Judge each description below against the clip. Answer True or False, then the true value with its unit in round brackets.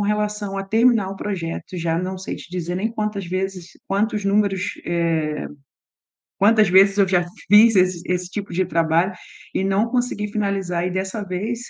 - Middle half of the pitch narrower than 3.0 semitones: True (2.6 semitones)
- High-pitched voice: True (195 Hz)